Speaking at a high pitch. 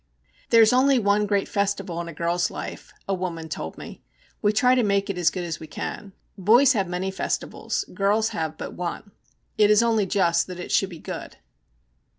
Yes: high, 195 Hz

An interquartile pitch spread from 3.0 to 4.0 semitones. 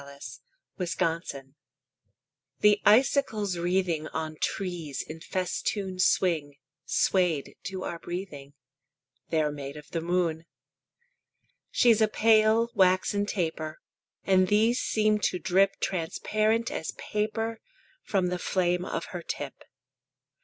No: average, 4.4 semitones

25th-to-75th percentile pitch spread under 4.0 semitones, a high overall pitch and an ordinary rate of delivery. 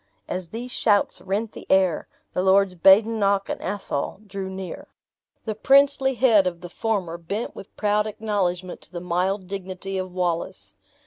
Yes: narrow, 2.6 semitones; high, 195 Hz; average, 155 wpm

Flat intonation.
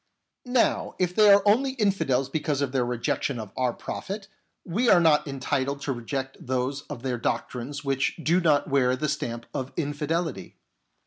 No: average, 4.7 semitones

